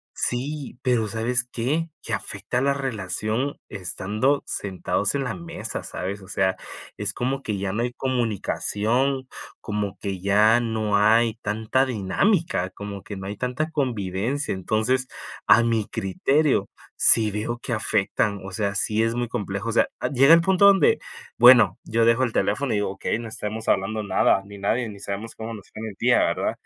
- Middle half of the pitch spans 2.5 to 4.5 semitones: Yes, average, 3.9 semitones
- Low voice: Yes, low, 110 Hz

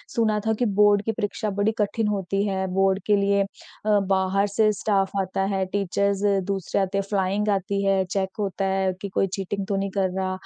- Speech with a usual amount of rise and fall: No, narrow, 1.1 semitones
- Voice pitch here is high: Yes, high, 195 Hz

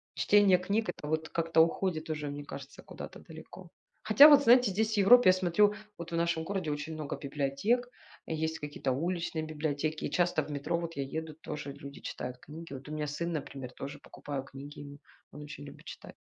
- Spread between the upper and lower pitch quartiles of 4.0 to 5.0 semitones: No, average, 3.5 semitones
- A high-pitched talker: No, medium, 155 Hz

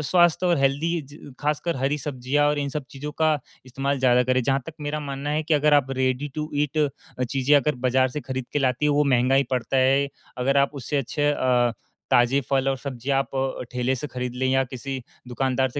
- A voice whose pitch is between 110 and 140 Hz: Yes, low, 135 Hz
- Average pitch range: No, narrow, 2.2 semitones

